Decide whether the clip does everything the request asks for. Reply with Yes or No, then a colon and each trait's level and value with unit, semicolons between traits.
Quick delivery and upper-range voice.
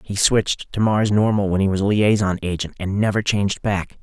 No: fast, 225 wpm; low, 100 Hz